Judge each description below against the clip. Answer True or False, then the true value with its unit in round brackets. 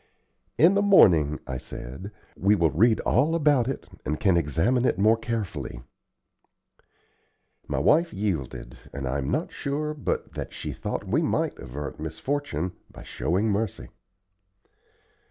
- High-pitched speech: False (100 Hz)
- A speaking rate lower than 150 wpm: True (140 wpm)